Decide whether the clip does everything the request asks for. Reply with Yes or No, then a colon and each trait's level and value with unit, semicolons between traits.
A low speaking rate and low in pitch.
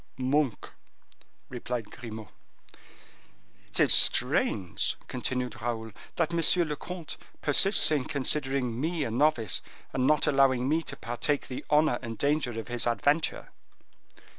Yes: slow, 130 wpm; low, 130 Hz